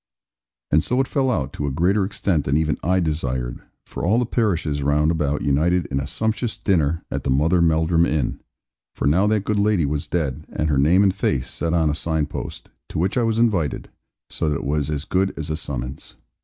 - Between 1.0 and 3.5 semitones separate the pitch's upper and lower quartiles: No, average, 4.8 semitones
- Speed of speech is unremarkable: No, fast, 220 wpm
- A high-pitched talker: No, very low, 80 Hz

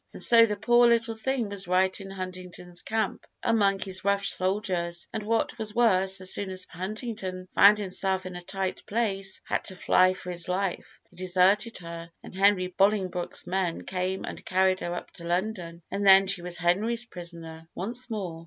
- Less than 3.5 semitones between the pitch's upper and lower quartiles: Yes, narrow, 2.5 semitones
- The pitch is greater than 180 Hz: Yes, high, 190 Hz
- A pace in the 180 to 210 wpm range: Yes, average, 190 wpm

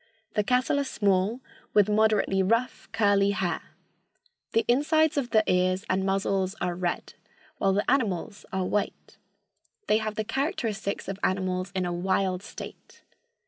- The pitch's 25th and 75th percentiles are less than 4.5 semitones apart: Yes, average, 3.1 semitones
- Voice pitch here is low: No, high, 200 Hz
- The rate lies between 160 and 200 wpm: No, average, 145 wpm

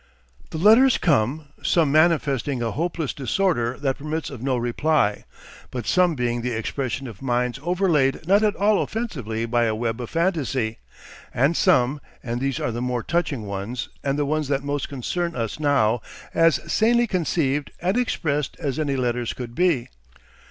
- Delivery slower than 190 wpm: Yes, average, 165 wpm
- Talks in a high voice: No, medium, 140 Hz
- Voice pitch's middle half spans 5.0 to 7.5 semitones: Yes, average, 5.3 semitones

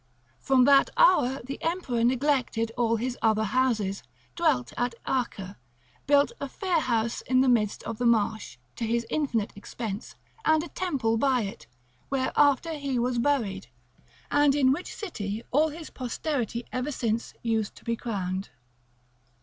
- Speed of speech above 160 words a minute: No, average, 155 wpm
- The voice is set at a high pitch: Yes, high, 245 Hz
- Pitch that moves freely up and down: No, average, 3.9 semitones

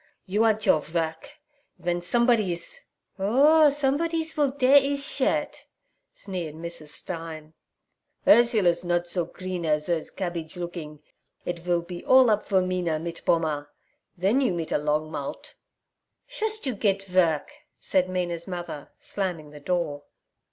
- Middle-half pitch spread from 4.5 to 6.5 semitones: Yes, wide, 5.4 semitones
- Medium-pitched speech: Yes, medium, 180 Hz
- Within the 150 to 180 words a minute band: No, average, 140 wpm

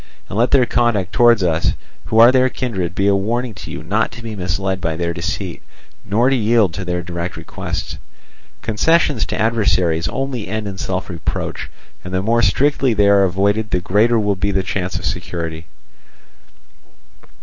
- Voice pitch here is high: No, low, 100 Hz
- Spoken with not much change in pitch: No, average, 4.4 semitones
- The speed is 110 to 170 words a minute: No, average, 180 wpm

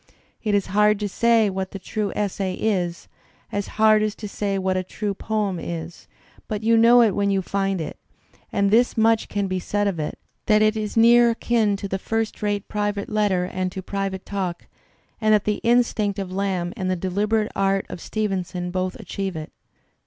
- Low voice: No, high, 200 Hz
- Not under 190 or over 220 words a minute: Yes, average, 195 wpm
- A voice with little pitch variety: Yes, narrow, 2.2 semitones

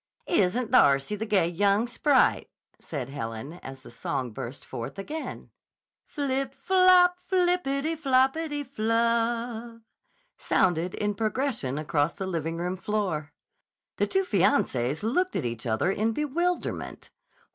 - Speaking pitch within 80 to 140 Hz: No, high, 215 Hz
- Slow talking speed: Yes, slow, 125 wpm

